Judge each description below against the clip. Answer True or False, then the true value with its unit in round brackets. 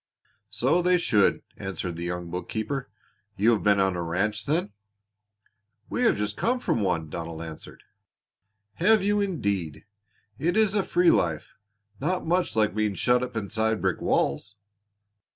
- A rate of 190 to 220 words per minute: False (150 wpm)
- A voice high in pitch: False (110 Hz)